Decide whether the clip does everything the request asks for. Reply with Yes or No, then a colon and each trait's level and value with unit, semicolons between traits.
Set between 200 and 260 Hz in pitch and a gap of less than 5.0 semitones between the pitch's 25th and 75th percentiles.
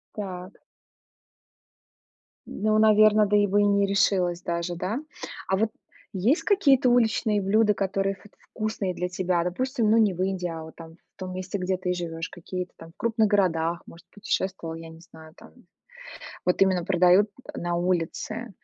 No: high, 190 Hz; average, 3.1 semitones